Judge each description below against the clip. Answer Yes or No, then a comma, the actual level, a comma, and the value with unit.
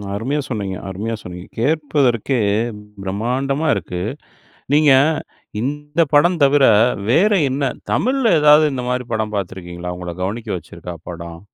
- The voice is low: Yes, low, 120 Hz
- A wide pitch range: Yes, wide, 7.6 semitones